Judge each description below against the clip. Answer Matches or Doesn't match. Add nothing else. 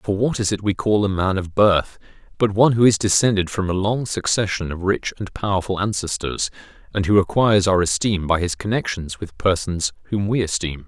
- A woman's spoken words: Doesn't match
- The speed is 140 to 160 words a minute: Doesn't match